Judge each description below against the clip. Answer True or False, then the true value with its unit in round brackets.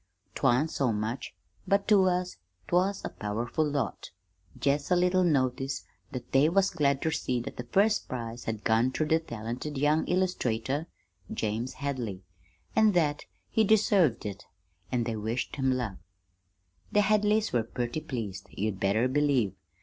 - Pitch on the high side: False (135 Hz)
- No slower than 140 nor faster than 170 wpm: True (155 wpm)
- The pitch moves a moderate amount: False (7.1 semitones)